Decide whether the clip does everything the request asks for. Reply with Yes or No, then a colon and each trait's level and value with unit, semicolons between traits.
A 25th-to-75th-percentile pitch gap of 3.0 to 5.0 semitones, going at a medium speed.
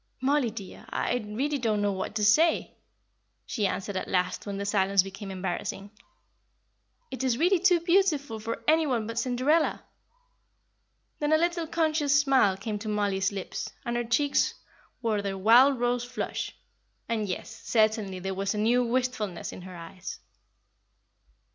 No: wide, 5.6 semitones; average, 155 wpm